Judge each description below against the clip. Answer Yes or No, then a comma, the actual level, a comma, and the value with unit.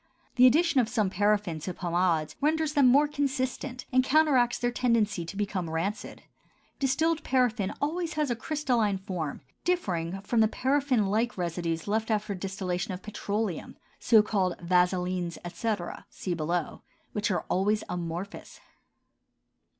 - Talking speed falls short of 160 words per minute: Yes, average, 140 wpm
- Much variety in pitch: Yes, wide, 6.1 semitones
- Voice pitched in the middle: No, high, 210 Hz